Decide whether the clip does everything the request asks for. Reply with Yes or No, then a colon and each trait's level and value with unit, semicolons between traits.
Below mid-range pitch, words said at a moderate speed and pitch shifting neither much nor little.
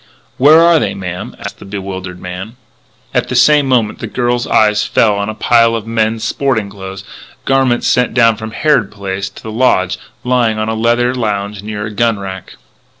Yes: low, 110 Hz; average, 190 wpm; average, 3.5 semitones